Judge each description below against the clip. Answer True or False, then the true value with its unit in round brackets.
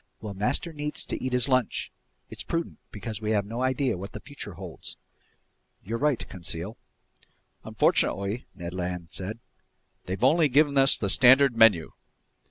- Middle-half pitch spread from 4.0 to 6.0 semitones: True (5.5 semitones)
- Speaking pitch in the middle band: False (115 Hz)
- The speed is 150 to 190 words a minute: True (155 wpm)